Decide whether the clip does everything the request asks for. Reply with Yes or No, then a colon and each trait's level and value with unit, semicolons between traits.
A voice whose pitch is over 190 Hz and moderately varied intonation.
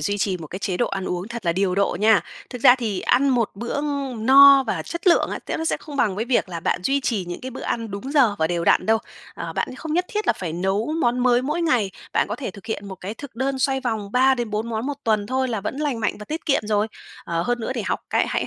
Yes: high, 230 Hz; average, 4.9 semitones